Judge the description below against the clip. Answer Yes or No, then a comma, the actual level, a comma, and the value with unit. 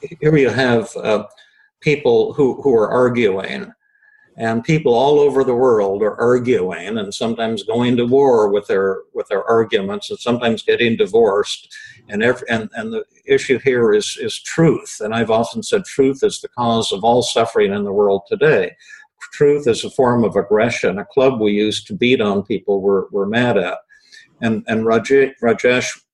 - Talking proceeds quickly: No, average, 180 wpm